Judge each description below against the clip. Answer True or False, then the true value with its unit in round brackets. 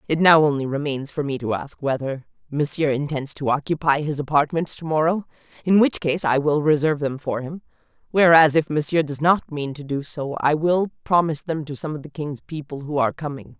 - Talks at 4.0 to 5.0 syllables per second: False (5.5 syllables/s)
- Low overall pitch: False (150 Hz)